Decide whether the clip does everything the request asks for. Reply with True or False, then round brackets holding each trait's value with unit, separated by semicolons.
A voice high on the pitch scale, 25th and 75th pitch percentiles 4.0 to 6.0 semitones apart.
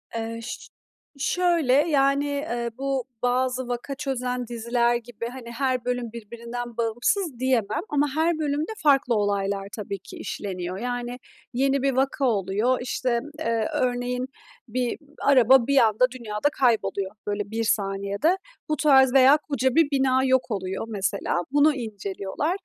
False (245 Hz; 3.4 semitones)